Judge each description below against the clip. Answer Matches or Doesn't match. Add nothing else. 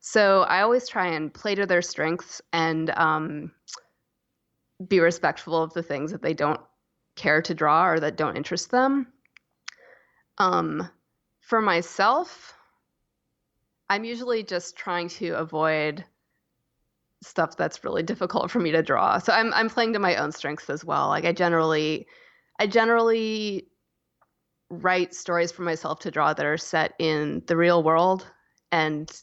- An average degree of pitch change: Matches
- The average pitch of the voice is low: Doesn't match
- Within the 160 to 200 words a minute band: Doesn't match